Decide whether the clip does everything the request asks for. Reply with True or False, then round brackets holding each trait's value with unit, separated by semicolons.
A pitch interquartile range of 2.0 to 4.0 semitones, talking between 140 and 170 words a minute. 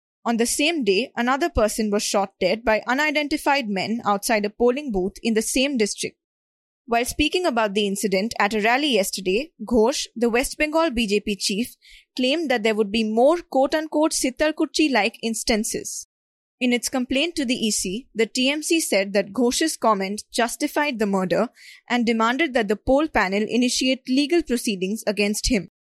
False (5.0 semitones; 165 wpm)